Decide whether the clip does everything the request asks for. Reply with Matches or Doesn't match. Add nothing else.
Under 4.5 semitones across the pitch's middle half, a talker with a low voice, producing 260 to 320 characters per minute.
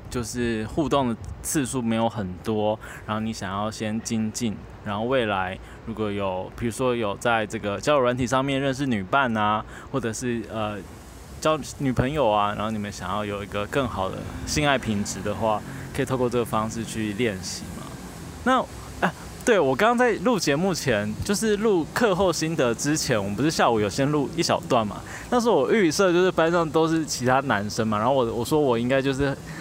Doesn't match